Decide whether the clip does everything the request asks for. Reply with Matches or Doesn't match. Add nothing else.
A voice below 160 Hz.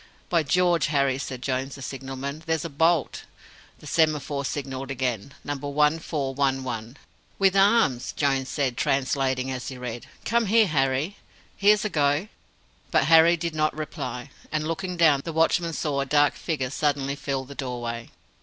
Matches